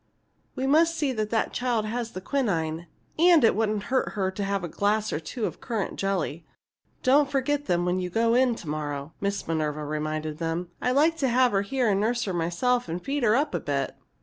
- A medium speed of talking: No, fast, 220 wpm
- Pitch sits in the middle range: No, high, 210 Hz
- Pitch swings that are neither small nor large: No, wide, 6.8 semitones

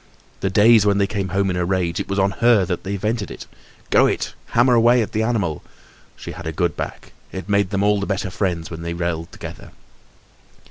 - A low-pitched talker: Yes, low, 100 Hz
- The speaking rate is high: Yes, fast, 225 wpm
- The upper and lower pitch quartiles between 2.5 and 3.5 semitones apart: Yes, average, 2.9 semitones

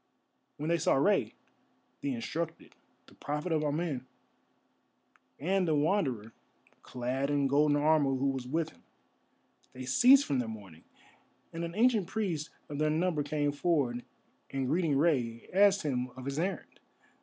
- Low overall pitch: No, medium, 150 Hz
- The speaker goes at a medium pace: Yes, average, 150 wpm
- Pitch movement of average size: Yes, average, 4.1 semitones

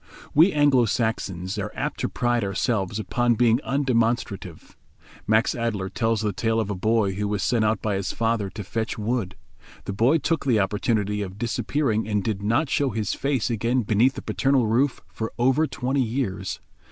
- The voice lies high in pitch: No, low, 115 Hz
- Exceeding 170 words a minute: Yes, average, 180 wpm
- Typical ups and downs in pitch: Yes, average, 3.2 semitones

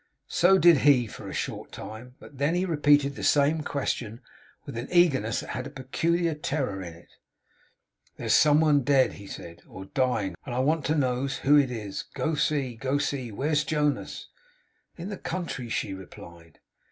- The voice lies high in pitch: No, medium, 140 Hz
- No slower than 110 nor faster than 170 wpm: No, average, 180 wpm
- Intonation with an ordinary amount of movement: Yes, average, 4.1 semitones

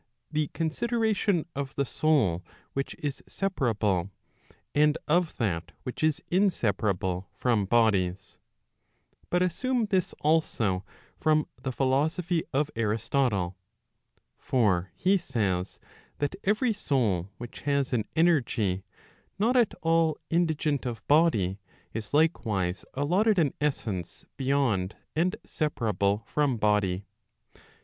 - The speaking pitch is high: No, low, 135 Hz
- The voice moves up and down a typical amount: No, wide, 7.9 semitones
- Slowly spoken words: Yes, slow, 110 wpm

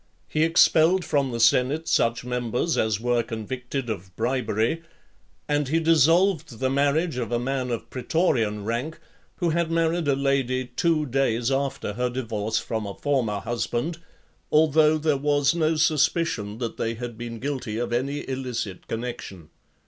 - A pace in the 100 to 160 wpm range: Yes, average, 155 wpm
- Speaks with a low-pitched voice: Yes, low, 130 Hz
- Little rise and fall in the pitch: No, average, 4.8 semitones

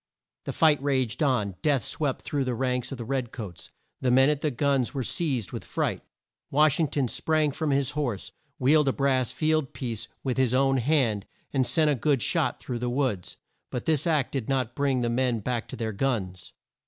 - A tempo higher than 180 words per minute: Yes, fast, 205 wpm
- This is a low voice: Yes, low, 130 Hz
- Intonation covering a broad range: No, average, 3.0 semitones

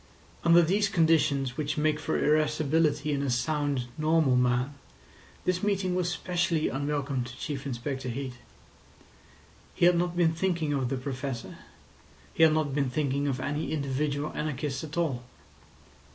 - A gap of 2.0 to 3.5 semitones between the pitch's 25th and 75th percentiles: Yes, average, 3.1 semitones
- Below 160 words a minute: Yes, average, 150 wpm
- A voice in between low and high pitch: Yes, medium, 150 Hz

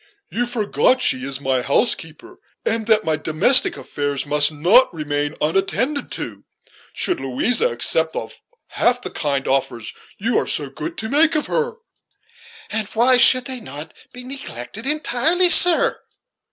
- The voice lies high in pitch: Yes, high, 220 Hz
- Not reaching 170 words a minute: Yes, average, 150 wpm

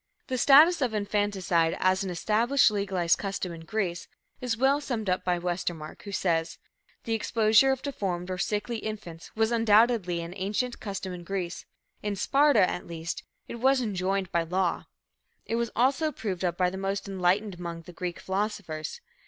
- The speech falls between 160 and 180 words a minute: Yes, average, 170 wpm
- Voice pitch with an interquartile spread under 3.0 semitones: No, average, 4.1 semitones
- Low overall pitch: No, high, 195 Hz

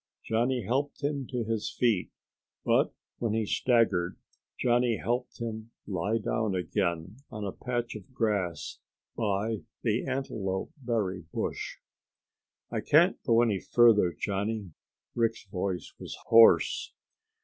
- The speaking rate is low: Yes, slow, 125 wpm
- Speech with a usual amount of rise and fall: Yes, average, 3.4 semitones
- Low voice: Yes, low, 110 Hz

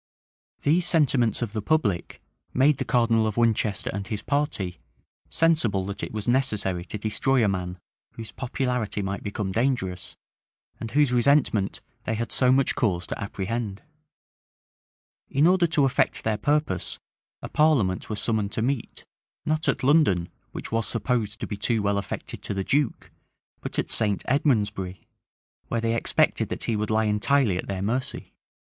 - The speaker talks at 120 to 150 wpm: No, average, 165 wpm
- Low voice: Yes, low, 115 Hz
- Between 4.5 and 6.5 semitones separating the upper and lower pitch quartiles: Yes, average, 4.9 semitones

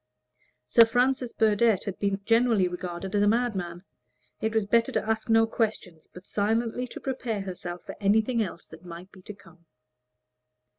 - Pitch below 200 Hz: No, high, 210 Hz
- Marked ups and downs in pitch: No, average, 3.8 semitones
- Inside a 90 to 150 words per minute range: No, average, 165 wpm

